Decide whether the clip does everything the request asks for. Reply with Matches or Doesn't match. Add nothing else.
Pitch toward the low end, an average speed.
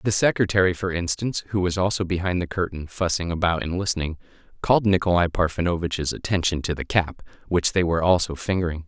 Matches